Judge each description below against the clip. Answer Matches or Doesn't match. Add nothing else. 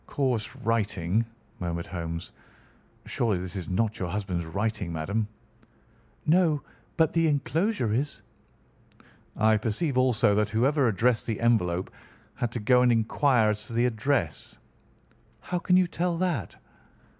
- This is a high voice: Doesn't match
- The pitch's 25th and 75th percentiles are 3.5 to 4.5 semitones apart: Doesn't match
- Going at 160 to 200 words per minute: Doesn't match